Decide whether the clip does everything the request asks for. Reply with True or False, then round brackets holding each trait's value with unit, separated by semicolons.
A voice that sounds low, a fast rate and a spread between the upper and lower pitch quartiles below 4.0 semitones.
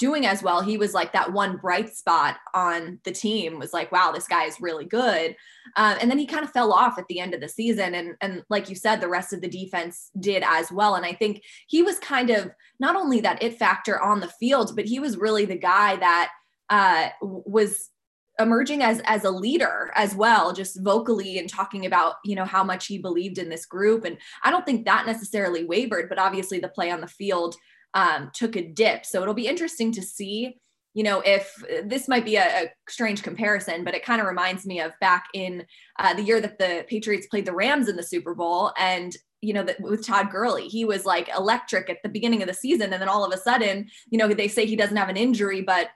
False (200 Hz; 240 wpm; 3.4 semitones)